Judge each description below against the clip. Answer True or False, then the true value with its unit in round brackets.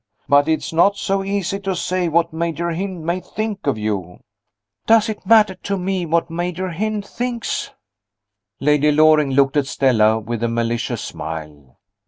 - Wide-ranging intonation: True (6.3 semitones)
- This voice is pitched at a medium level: True (165 Hz)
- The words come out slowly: False (160 wpm)